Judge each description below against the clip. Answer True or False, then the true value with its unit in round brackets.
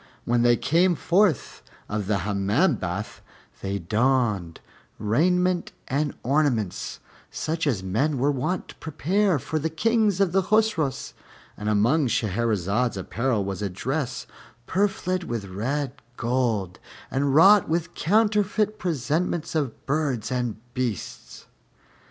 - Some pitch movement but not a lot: False (7.8 semitones)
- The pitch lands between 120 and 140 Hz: True (135 Hz)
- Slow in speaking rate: True (120 wpm)